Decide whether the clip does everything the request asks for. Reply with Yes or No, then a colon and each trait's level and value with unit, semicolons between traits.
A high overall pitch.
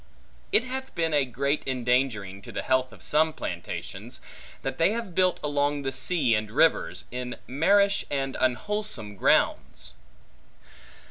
No: low, 135 Hz